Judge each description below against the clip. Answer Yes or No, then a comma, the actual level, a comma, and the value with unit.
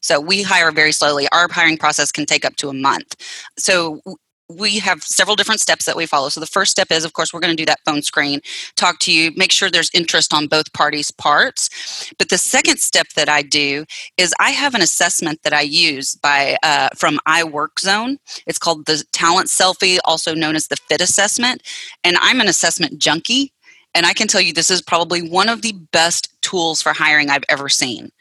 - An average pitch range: Yes, average, 3.8 semitones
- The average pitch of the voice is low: No, medium, 165 Hz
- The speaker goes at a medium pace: No, fast, 215 wpm